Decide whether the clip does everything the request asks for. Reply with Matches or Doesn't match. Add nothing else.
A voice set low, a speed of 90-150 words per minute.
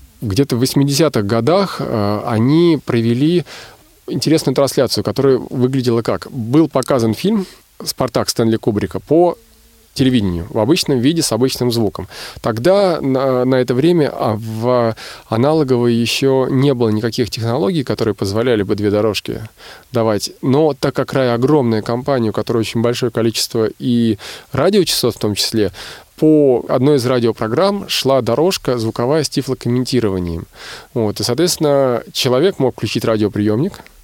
Matches